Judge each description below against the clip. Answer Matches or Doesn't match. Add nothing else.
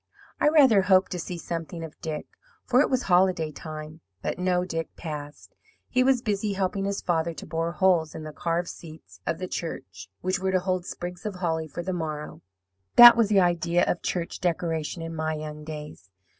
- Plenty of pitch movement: Doesn't match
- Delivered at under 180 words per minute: Doesn't match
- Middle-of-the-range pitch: Matches